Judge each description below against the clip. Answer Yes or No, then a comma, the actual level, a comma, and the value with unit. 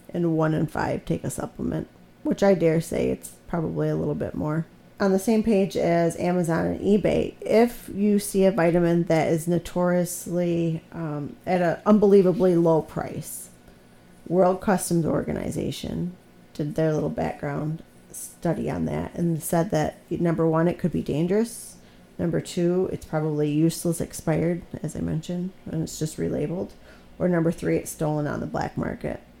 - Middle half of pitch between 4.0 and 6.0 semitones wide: No, average, 3.3 semitones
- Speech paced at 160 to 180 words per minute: Yes, average, 165 wpm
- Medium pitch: Yes, medium, 165 Hz